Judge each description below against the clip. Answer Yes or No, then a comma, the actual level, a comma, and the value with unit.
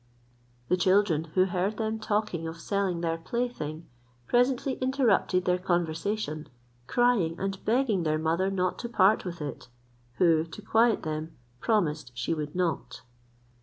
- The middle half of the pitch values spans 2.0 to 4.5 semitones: No, average, 5.0 semitones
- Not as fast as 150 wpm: Yes, average, 140 wpm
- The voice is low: No, medium, 185 Hz